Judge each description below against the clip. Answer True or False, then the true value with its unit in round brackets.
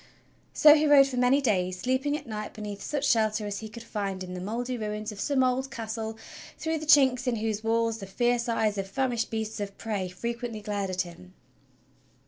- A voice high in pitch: True (225 Hz)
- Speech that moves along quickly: True (210 wpm)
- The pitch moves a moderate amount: True (3.4 semitones)